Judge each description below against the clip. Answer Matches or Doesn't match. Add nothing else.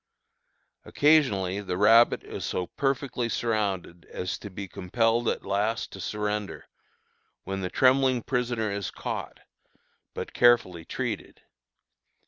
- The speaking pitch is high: Doesn't match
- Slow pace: Matches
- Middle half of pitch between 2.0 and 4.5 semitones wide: Matches